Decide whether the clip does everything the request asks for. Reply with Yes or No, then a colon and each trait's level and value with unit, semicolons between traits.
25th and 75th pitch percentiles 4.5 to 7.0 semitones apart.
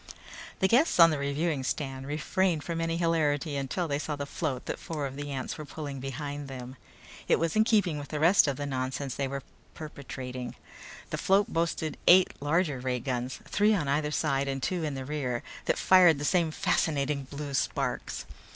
No: average, 3.4 semitones